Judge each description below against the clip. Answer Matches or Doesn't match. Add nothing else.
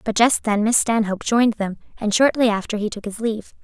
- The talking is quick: Matches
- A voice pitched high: Matches